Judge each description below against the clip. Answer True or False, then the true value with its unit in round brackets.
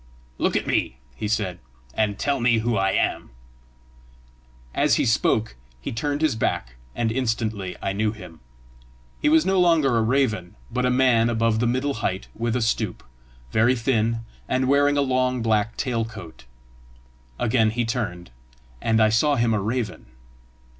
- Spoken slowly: False (165 wpm)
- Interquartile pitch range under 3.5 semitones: True (2.9 semitones)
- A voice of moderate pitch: False (115 Hz)